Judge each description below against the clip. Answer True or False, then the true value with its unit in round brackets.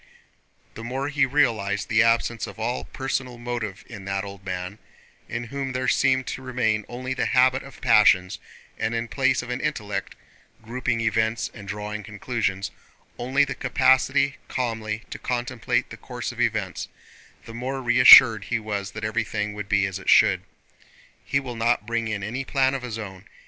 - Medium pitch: False (115 Hz)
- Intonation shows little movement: False (3.5 semitones)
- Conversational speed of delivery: True (170 wpm)